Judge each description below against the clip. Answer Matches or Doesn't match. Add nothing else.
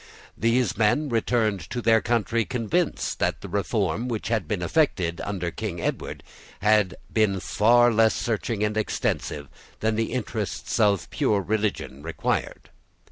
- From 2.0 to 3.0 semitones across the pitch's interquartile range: Matches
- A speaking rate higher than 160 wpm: Doesn't match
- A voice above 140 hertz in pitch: Doesn't match